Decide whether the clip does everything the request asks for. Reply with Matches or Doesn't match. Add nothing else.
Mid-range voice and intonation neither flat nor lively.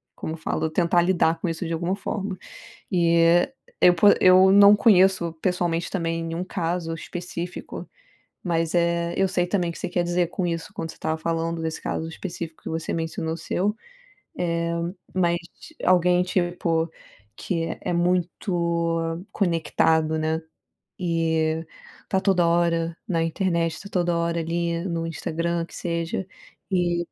Doesn't match